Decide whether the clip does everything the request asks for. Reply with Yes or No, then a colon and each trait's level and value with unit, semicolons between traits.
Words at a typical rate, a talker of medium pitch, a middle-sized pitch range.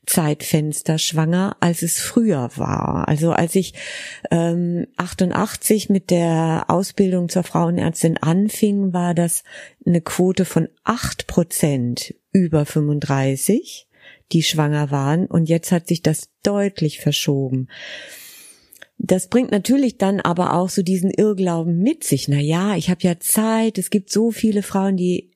Yes: average, 135 wpm; medium, 175 Hz; average, 3.4 semitones